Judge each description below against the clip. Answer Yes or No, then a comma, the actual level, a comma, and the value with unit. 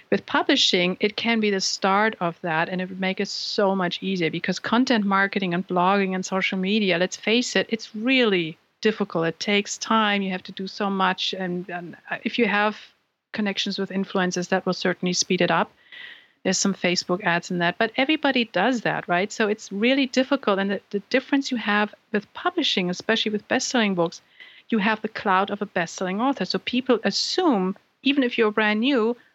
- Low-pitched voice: No, high, 200 Hz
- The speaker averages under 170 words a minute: No, average, 200 wpm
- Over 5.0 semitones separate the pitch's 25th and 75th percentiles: No, average, 3.8 semitones